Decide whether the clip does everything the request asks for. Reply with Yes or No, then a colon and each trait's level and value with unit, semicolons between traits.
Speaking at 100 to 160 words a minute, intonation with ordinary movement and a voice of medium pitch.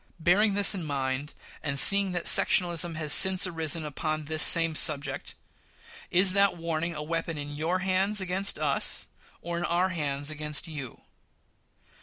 Yes: average, 155 wpm; average, 3.4 semitones; medium, 165 Hz